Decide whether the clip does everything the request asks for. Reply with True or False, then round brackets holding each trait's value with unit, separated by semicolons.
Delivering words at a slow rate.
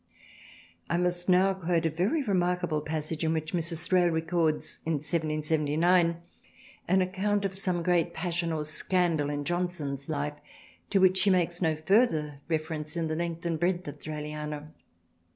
False (155 wpm)